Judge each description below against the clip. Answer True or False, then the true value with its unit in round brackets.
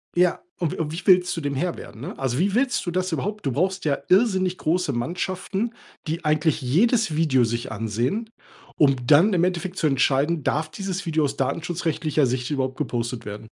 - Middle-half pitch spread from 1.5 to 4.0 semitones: False (5.3 semitones)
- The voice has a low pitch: False (160 Hz)